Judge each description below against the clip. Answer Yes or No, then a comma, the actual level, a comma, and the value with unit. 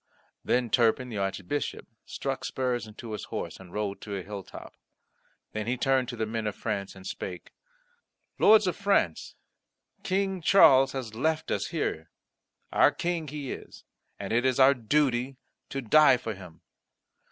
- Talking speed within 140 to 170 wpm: Yes, average, 160 wpm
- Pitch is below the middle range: Yes, low, 120 Hz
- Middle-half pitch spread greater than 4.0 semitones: Yes, average, 4.9 semitones